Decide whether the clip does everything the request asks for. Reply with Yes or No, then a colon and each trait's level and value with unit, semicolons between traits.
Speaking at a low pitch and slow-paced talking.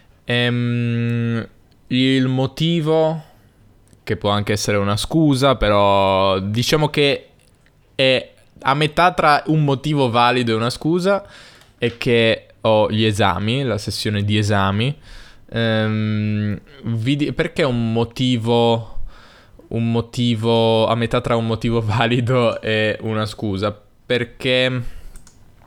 Yes: low, 115 Hz; slow, 110 wpm